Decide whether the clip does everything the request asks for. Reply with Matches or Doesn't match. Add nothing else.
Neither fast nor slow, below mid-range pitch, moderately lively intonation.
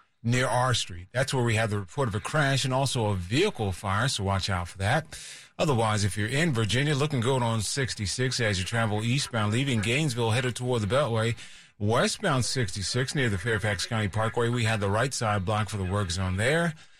Doesn't match